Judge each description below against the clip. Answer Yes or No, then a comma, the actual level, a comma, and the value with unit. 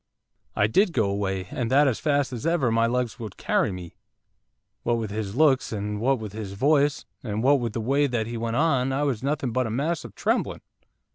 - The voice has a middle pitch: No, low, 120 Hz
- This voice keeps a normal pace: No, fast, 220 wpm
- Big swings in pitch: No, average, 4.3 semitones